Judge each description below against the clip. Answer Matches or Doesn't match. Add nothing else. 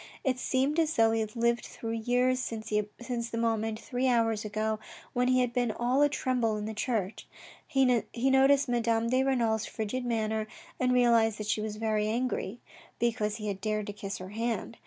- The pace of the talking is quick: Doesn't match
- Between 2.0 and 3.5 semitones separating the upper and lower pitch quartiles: Matches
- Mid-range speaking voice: Doesn't match